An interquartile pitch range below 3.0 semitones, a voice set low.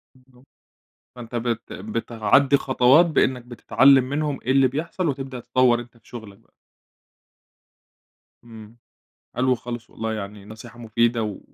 Yes: narrow, 2.6 semitones; low, 120 Hz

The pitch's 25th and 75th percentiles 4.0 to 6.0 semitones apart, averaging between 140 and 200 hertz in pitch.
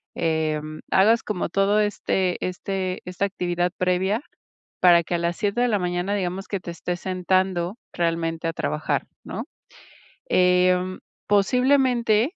No: narrow, 2.5 semitones; medium, 185 Hz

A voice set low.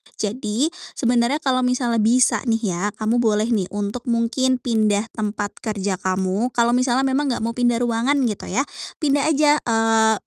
No: high, 235 Hz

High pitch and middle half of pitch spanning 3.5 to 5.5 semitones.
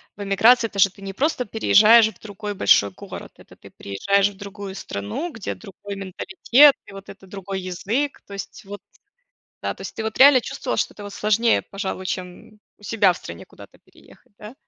No: high, 200 Hz; narrow, 2.4 semitones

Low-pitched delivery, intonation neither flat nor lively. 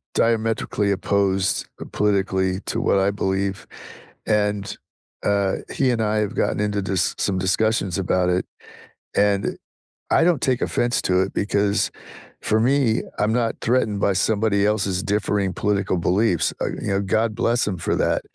No: low, 100 Hz; narrow, 2.3 semitones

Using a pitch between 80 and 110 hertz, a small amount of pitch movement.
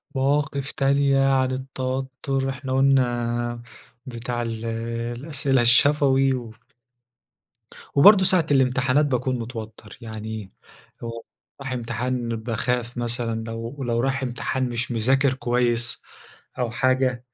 No: low, 125 Hz; narrow, 2.3 semitones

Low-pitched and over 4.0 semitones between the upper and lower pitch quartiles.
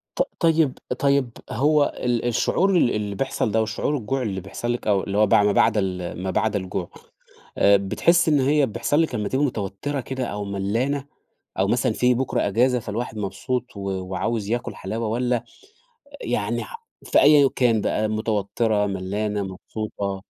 Yes: low, 110 Hz; average, 4.5 semitones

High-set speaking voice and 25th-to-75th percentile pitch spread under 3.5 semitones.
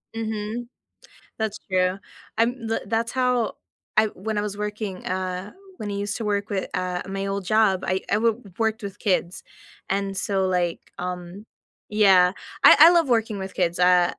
Yes: high, 200 Hz; average, 2.9 semitones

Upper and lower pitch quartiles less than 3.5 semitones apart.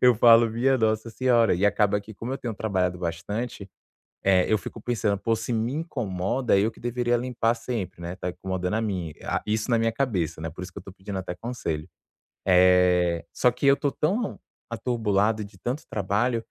No: average, 4.3 semitones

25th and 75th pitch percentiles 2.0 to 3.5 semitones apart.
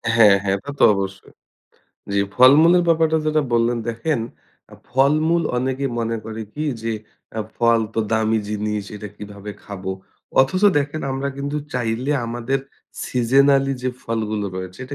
No: average, 4.4 semitones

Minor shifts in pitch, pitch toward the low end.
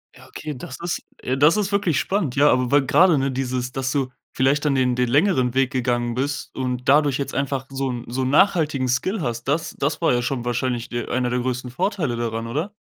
No: average, 3.0 semitones; low, 130 Hz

